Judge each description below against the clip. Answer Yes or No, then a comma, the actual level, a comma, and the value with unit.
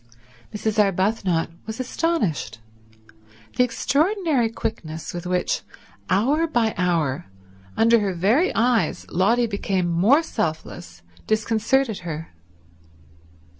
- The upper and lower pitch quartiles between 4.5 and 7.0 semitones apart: Yes, wide, 5.6 semitones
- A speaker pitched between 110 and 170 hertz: No, high, 215 Hz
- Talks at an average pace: No, slow, 95 wpm